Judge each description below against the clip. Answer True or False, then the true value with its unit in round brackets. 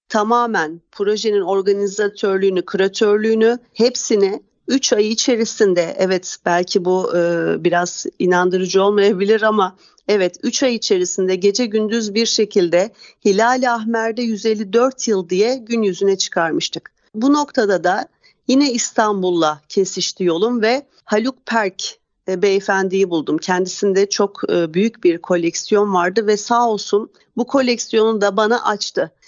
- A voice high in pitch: True (210 Hz)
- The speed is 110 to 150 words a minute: True (125 wpm)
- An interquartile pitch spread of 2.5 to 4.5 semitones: True (3.3 semitones)